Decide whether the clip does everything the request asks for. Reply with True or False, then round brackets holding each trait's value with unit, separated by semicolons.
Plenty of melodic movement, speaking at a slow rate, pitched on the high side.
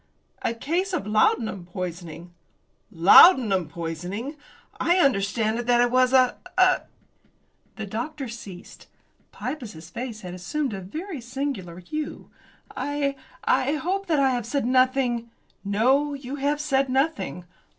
True (6.2 semitones; 130 wpm; 245 Hz)